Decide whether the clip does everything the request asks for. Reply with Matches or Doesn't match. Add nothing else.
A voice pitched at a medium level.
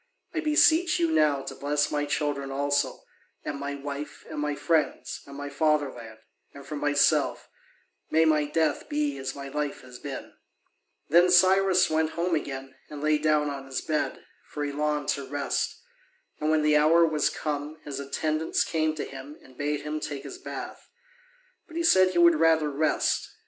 Matches